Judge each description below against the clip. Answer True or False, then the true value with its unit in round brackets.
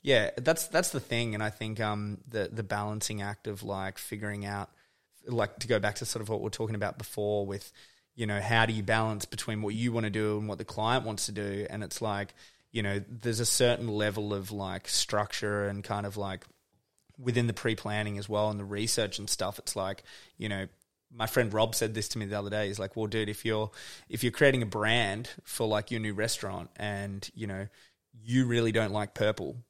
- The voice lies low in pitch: True (105 Hz)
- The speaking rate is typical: False (230 wpm)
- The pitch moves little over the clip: True (1.8 semitones)